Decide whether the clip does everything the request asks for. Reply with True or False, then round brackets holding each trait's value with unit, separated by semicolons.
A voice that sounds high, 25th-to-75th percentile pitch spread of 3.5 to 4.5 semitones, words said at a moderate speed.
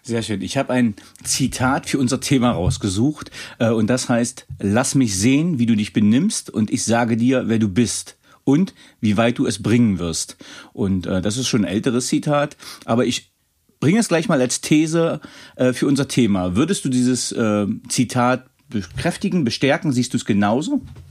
False (125 Hz; 4.0 semitones; 175 wpm)